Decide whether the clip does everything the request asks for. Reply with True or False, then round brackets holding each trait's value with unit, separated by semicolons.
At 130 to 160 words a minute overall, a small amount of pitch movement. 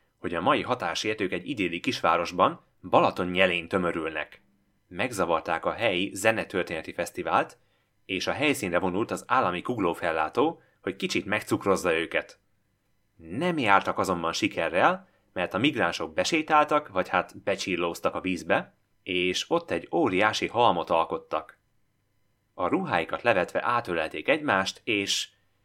False (115 wpm; 1.8 semitones)